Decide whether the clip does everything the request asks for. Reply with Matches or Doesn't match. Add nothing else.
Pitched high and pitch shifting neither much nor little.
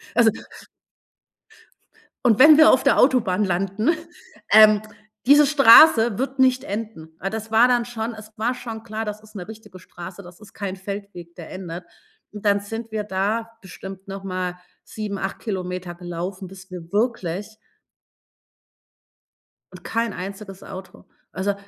Matches